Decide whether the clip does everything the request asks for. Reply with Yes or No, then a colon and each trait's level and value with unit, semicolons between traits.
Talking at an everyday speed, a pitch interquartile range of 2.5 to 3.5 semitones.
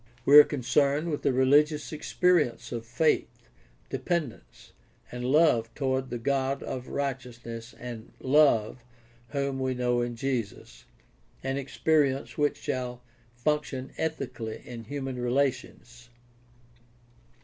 No: slow, 120 wpm; average, 2.8 semitones